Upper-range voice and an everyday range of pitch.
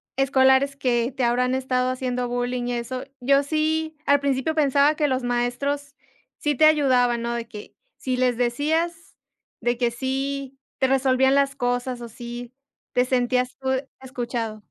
No: very high, 255 Hz; narrow, 2.3 semitones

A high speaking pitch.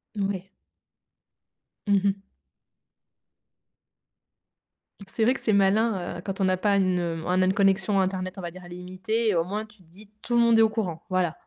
Yes: high, 195 Hz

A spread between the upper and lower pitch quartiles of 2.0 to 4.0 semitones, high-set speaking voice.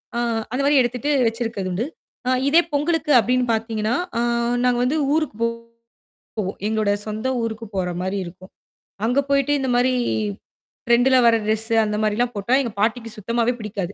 Yes: average, 3.1 semitones; high, 230 Hz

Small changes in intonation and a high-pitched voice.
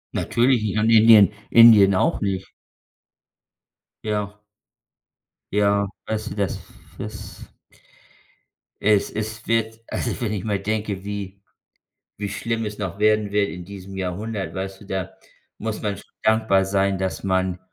No: narrow, 2.1 semitones; low, 105 Hz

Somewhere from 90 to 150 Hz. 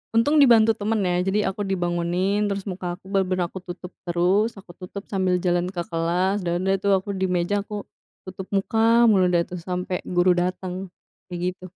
No: medium, 185 Hz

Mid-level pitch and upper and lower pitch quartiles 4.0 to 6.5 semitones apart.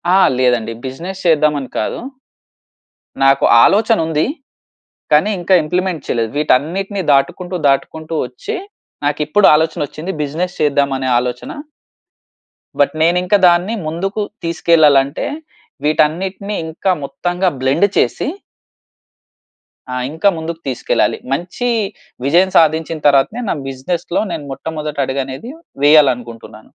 Yes: medium, 155 Hz; average, 4.5 semitones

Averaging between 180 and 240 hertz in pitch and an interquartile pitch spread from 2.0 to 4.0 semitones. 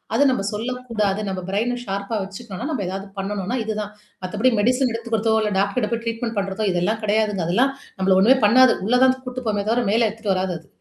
Yes: high, 215 Hz; average, 3.4 semitones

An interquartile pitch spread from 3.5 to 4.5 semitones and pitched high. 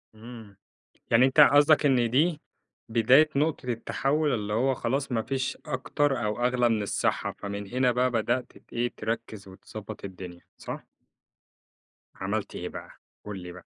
No: average, 3.8 semitones; low, 120 Hz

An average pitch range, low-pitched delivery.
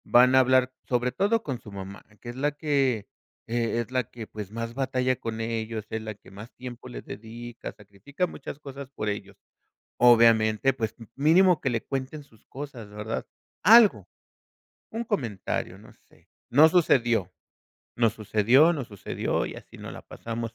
Yes: average, 3.7 semitones; low, 120 Hz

